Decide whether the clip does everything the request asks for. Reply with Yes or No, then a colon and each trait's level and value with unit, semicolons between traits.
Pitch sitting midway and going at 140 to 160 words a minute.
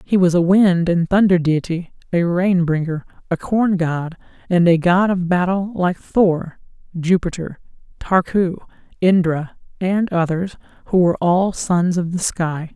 Yes: medium, 175 Hz; average, 150 wpm